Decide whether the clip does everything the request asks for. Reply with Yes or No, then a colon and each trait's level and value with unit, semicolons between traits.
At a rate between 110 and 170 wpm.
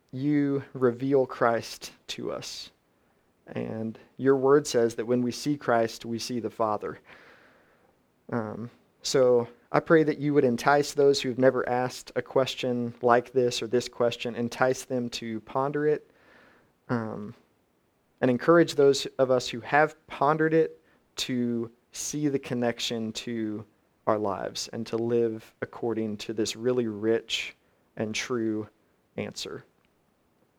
Yes: average, 140 wpm